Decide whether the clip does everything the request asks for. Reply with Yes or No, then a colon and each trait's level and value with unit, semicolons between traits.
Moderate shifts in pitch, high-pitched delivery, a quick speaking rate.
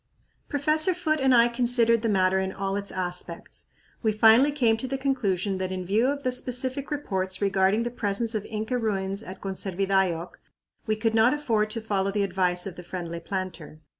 No: average, 4.4 semitones; high, 210 Hz; average, 190 wpm